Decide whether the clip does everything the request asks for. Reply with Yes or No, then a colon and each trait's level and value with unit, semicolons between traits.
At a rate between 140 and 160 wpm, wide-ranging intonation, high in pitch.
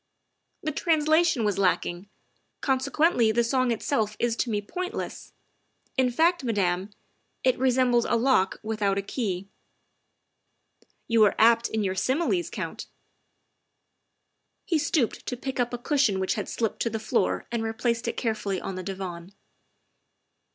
No: average, 155 wpm; average, 4.3 semitones; high, 235 Hz